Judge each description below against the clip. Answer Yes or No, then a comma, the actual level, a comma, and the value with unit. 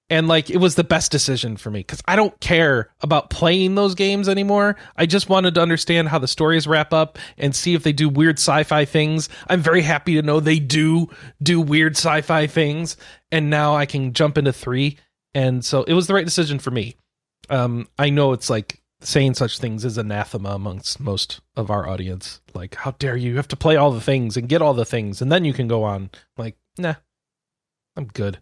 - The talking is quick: Yes, fast, 220 wpm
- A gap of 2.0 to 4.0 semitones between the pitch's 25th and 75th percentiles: No, average, 4.9 semitones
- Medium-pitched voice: Yes, medium, 150 Hz